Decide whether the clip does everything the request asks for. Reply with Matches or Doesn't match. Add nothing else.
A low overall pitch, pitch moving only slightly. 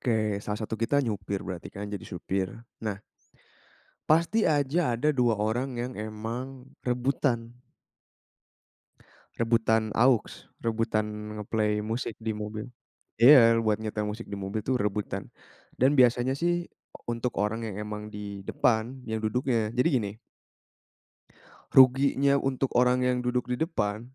Doesn't match